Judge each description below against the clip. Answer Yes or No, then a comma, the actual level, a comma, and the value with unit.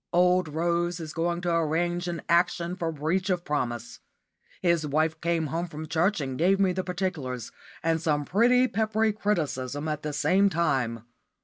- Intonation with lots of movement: No, average, 3.0 semitones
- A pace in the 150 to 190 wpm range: Yes, average, 170 wpm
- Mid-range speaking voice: Yes, medium, 170 Hz